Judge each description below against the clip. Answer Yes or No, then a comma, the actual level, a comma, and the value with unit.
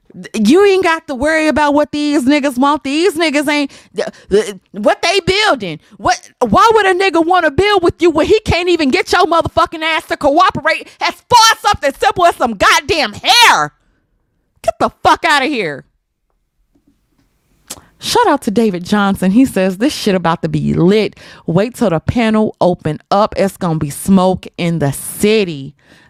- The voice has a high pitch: Yes, very high, 290 Hz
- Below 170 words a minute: No, average, 175 wpm